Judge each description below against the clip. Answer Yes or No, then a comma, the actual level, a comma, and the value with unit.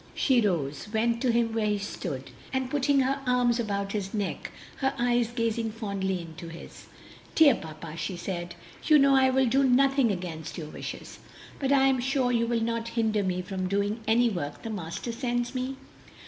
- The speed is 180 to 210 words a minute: Yes, average, 190 wpm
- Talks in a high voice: Yes, high, 230 Hz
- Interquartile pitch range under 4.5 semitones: No, average, 4.9 semitones